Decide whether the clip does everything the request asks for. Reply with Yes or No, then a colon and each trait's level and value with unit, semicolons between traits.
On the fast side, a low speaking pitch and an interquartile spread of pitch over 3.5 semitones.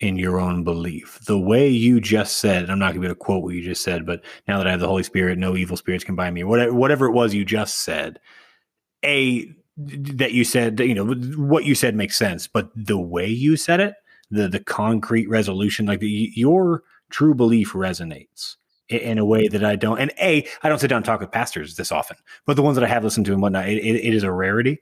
Yes: fast, 245 wpm; low, 110 Hz; average, 4.7 semitones